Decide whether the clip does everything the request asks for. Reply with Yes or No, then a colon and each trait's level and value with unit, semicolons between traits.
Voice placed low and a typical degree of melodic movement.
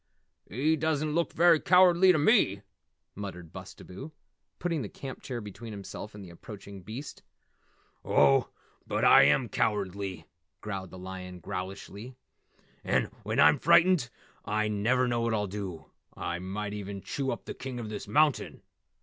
No: low, 105 Hz; wide, 6.0 semitones